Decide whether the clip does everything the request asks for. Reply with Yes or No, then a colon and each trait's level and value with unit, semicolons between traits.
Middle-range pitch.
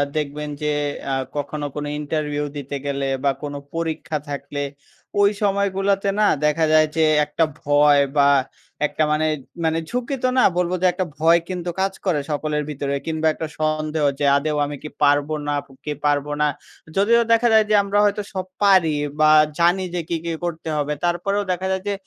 Yes: medium, 155 Hz